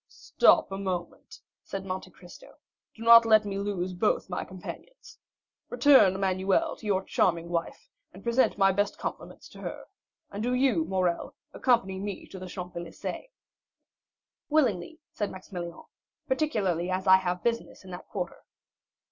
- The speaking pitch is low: No, high, 195 Hz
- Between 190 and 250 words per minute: No, average, 150 wpm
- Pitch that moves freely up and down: No, average, 3.8 semitones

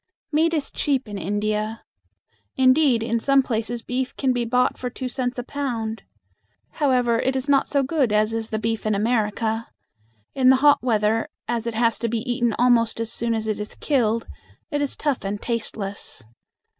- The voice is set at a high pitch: Yes, high, 235 Hz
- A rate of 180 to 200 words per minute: Yes, average, 185 wpm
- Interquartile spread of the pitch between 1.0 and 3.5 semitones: Yes, average, 2.9 semitones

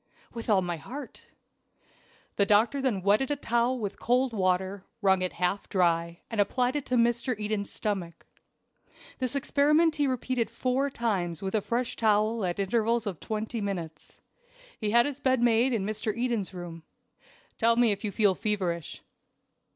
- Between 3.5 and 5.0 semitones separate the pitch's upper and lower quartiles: Yes, average, 4.2 semitones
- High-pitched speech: Yes, high, 220 Hz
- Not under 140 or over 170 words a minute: Yes, average, 165 wpm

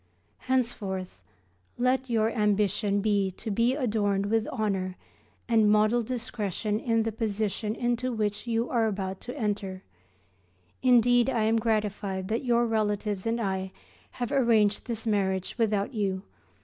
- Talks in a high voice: Yes, high, 215 Hz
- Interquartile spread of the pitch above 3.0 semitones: No, narrow, 2.6 semitones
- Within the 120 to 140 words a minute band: Yes, slow, 135 wpm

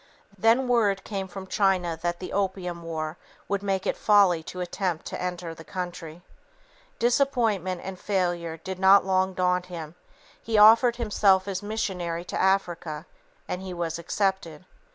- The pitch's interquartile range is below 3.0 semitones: Yes, narrow, 2.5 semitones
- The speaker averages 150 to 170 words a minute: Yes, average, 155 wpm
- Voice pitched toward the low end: No, medium, 185 Hz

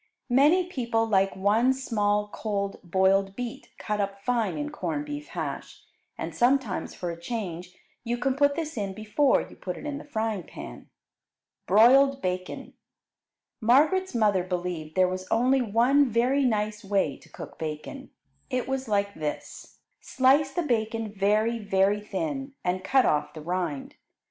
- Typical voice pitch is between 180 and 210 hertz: No, high, 220 Hz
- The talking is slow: No, average, 155 wpm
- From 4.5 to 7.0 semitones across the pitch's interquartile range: Yes, wide, 5.6 semitones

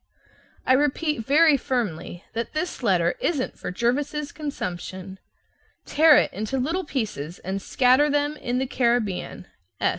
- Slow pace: Yes, slow, 130 wpm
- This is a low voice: No, very high, 255 Hz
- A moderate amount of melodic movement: No, wide, 7.0 semitones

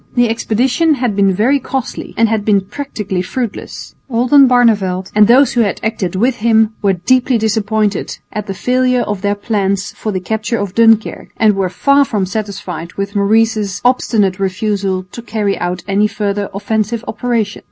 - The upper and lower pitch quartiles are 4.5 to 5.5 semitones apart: No, average, 3.1 semitones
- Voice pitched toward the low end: No, high, 215 Hz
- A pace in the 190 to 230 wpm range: No, average, 165 wpm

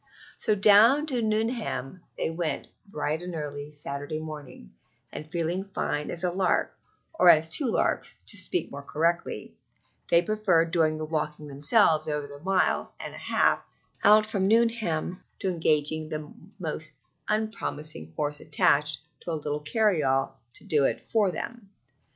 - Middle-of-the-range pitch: Yes, medium, 160 Hz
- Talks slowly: No, average, 155 wpm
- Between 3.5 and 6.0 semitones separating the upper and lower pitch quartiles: Yes, average, 5.1 semitones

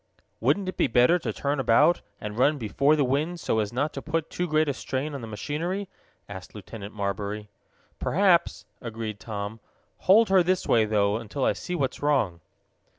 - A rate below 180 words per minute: No, average, 185 wpm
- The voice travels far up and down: Yes, wide, 6.9 semitones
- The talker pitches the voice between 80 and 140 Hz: Yes, low, 135 Hz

